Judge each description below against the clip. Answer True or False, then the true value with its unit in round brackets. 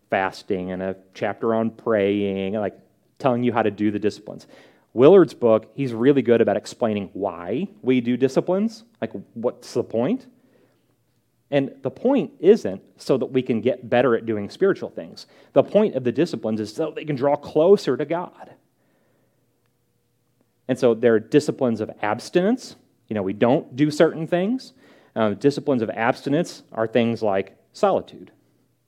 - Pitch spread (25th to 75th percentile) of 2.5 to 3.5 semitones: False (5.3 semitones)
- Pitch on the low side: True (125 Hz)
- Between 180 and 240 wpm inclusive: False (160 wpm)